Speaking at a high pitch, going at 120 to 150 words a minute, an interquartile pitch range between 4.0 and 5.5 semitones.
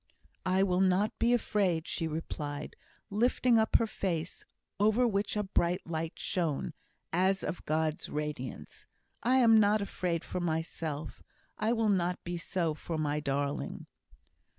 No: medium, 180 Hz; average, 145 wpm; average, 4.8 semitones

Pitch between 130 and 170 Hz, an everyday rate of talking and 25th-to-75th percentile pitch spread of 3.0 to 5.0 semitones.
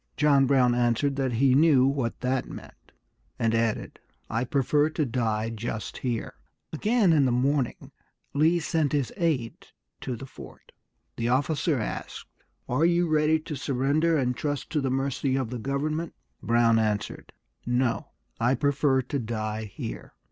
Yes: low, 135 Hz; average, 155 wpm; average, 3.9 semitones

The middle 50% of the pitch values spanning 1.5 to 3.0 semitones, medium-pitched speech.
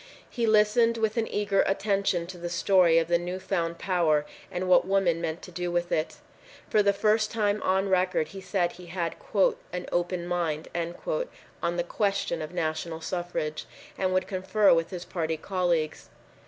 Yes: narrow, 2.6 semitones; medium, 180 Hz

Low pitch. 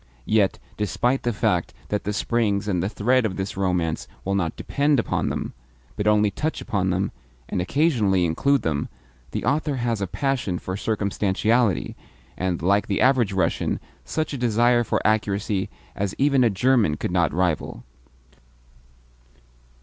Yes: low, 105 Hz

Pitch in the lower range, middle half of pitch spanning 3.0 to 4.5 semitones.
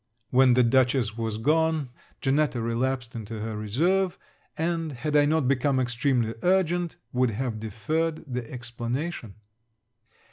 No: low, 130 Hz; average, 5.0 semitones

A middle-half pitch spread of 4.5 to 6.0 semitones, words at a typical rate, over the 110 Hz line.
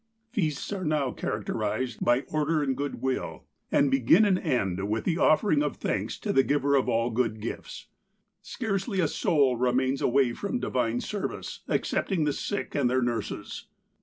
Yes: average, 4.8 semitones; average, 170 wpm; low, 135 Hz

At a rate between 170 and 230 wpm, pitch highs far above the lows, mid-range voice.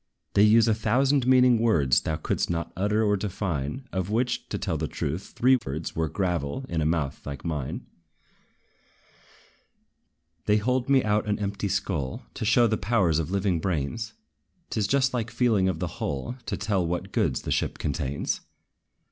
No: average, 175 wpm; wide, 6.0 semitones; low, 100 Hz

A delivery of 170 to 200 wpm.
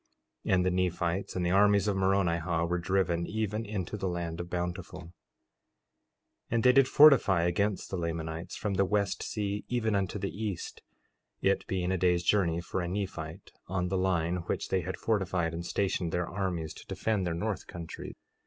Yes: average, 190 wpm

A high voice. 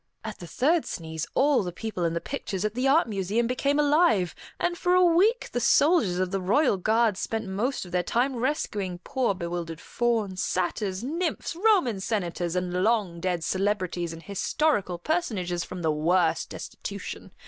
Yes: high, 205 Hz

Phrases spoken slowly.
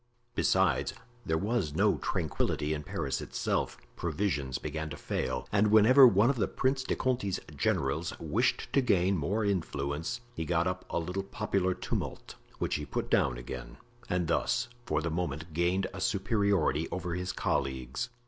No: average, 160 wpm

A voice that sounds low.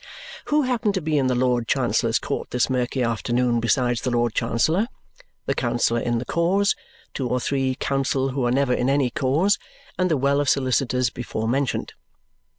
Yes: low, 130 Hz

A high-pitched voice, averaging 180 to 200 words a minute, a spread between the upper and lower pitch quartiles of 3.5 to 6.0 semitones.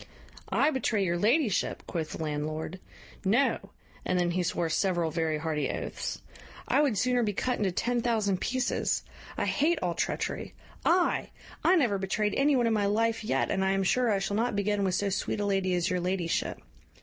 Yes: high, 200 Hz; average, 195 wpm; average, 4.7 semitones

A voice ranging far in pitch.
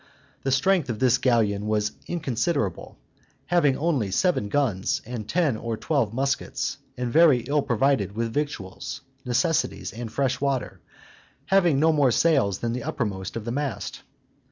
No: average, 4.8 semitones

